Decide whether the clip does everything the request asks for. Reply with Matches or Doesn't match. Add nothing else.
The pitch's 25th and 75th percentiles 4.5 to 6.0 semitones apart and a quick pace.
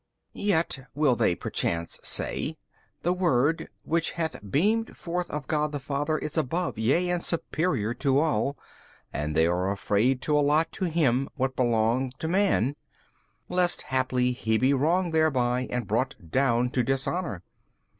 Doesn't match